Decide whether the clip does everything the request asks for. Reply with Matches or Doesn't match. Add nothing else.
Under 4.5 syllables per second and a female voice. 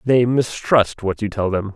Doesn't match